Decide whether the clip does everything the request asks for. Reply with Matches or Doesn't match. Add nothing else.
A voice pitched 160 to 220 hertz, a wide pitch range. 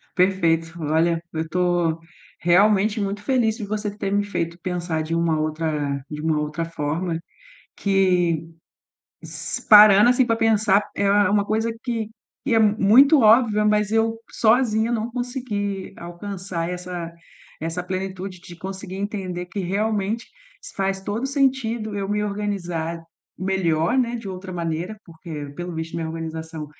Doesn't match